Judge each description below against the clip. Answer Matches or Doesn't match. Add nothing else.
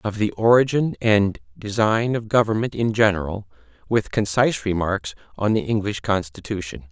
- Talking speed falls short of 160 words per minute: Matches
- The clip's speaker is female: Doesn't match